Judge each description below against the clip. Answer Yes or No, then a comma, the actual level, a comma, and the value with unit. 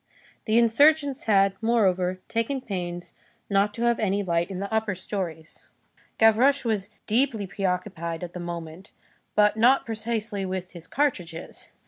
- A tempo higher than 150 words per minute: No, average, 140 wpm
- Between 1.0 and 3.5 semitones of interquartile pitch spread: No, average, 4.0 semitones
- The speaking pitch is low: No, high, 200 Hz